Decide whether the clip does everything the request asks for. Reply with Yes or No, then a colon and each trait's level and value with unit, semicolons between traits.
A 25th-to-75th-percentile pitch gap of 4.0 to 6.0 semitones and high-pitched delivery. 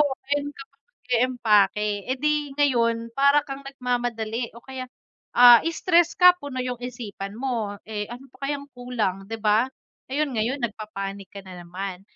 Yes: average, 4.4 semitones; high, 245 Hz